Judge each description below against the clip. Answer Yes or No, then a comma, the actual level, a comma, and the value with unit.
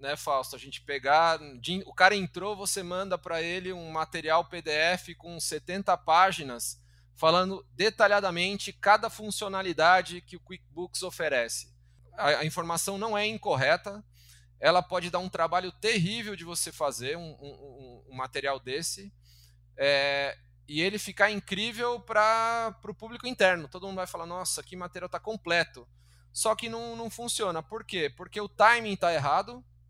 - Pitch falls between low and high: Yes, medium, 175 Hz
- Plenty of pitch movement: Yes, wide, 5.9 semitones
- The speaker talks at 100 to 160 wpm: Yes, average, 155 wpm